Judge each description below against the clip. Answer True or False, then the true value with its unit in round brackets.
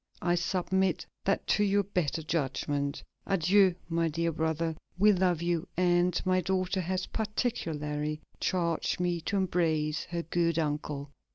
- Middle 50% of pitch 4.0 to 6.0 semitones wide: False (2.7 semitones)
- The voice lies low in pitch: False (170 Hz)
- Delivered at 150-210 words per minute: False (140 wpm)